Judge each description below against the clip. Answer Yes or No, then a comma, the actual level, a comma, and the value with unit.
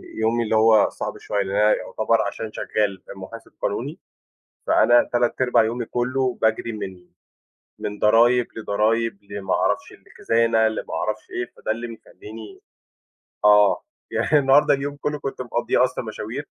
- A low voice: Yes, low, 115 Hz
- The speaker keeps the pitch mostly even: Yes, narrow, 2.2 semitones